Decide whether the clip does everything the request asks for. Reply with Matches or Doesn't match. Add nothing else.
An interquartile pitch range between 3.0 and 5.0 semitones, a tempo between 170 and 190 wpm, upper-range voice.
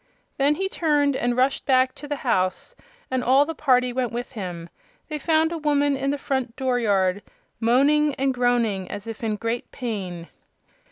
Matches